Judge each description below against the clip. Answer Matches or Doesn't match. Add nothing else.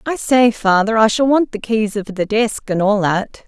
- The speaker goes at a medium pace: Doesn't match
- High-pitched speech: Matches